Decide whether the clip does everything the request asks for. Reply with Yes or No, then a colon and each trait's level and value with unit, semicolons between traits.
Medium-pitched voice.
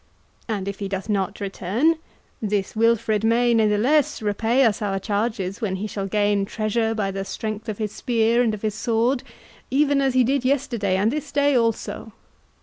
No: high, 220 Hz